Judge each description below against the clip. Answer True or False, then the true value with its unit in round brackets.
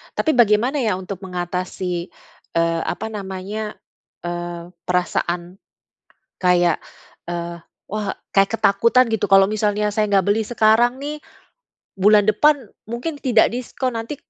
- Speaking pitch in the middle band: False (205 Hz)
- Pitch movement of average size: True (4.2 semitones)